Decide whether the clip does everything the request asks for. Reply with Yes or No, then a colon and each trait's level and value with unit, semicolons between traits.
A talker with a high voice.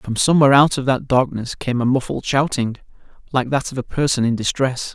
No: low, 130 Hz